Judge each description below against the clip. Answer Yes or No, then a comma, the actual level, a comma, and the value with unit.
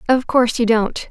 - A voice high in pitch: Yes, high, 235 Hz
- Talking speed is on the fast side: Yes, fast, 215 wpm